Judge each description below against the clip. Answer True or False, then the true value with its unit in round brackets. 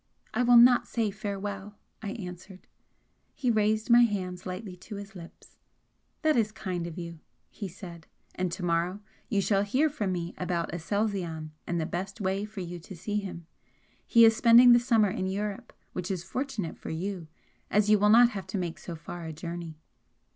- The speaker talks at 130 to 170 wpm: False (190 wpm)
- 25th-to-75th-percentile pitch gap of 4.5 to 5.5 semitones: False (3.4 semitones)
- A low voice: False (195 Hz)